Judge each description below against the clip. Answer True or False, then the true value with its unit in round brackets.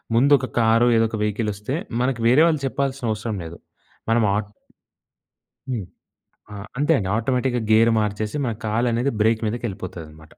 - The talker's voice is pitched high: False (115 Hz)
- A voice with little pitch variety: False (3.0 semitones)